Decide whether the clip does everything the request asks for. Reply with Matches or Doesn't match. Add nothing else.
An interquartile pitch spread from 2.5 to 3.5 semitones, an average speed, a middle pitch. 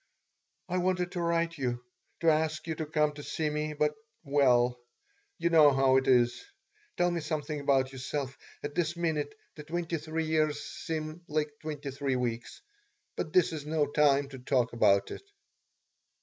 Matches